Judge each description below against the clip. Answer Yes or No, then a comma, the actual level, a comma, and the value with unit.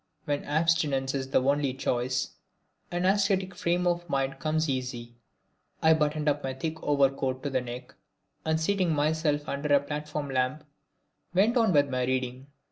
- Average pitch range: Yes, average, 3.3 semitones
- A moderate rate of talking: Yes, average, 160 wpm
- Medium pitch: Yes, medium, 145 Hz